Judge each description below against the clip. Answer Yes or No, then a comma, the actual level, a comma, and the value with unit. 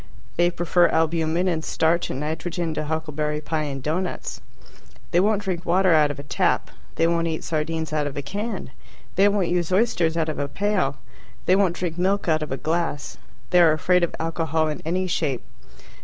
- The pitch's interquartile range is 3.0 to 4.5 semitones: No, narrow, 2.6 semitones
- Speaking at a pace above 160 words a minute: Yes, average, 195 wpm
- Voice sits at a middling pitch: Yes, medium, 165 Hz